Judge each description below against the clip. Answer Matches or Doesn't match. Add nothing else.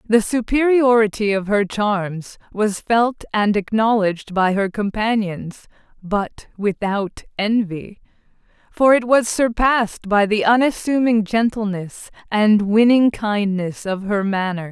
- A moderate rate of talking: Doesn't match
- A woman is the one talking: Matches